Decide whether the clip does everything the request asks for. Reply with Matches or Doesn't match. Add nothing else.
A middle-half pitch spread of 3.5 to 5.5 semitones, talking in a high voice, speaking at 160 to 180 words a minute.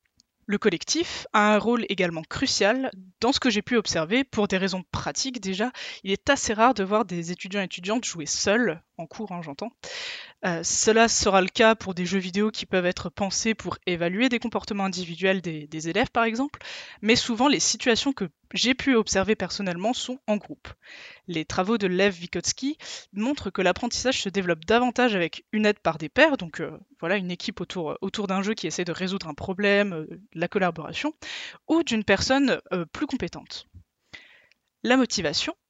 Doesn't match